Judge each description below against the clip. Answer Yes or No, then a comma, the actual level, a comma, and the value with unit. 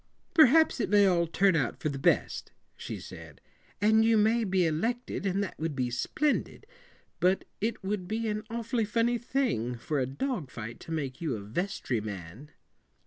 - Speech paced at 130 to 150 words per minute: No, average, 180 wpm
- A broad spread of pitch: Yes, wide, 8.6 semitones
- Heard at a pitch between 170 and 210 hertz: Yes, high, 190 Hz